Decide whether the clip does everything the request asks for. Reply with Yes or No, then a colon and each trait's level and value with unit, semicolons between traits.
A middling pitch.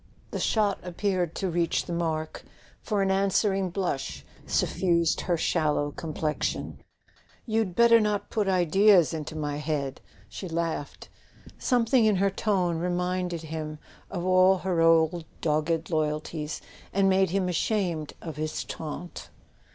Yes: medium, 175 Hz